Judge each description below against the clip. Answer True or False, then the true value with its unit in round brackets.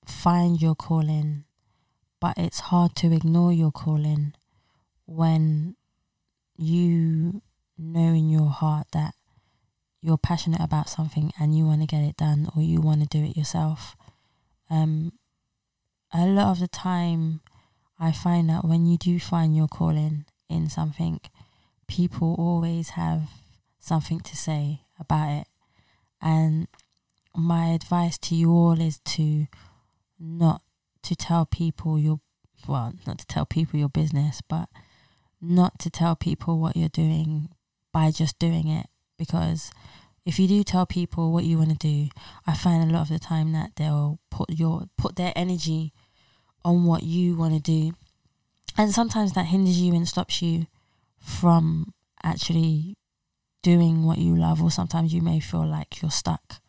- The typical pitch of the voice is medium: True (160 Hz)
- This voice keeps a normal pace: True (155 wpm)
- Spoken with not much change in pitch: True (1.9 semitones)